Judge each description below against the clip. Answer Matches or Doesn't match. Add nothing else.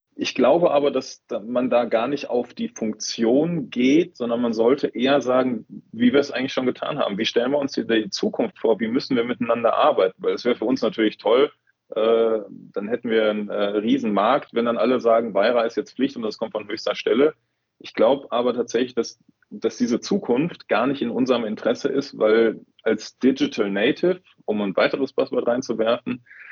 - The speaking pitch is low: Matches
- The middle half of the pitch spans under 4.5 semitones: Doesn't match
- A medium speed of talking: Doesn't match